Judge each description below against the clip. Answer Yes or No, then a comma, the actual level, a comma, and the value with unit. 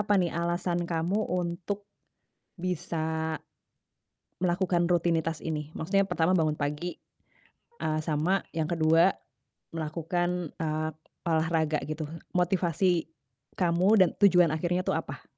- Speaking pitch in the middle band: Yes, medium, 170 Hz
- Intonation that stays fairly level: Yes, narrow, 2.0 semitones